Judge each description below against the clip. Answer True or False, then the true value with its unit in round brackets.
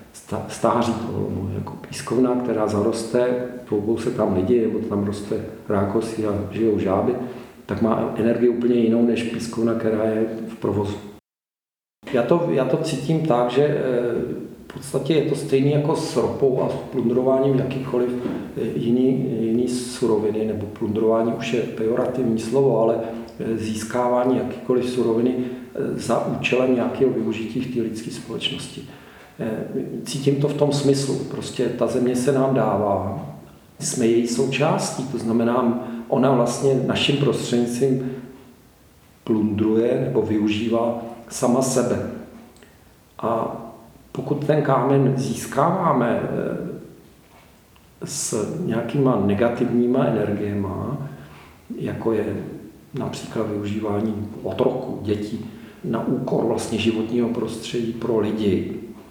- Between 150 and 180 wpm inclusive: False (115 wpm)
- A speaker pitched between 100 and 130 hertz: True (120 Hz)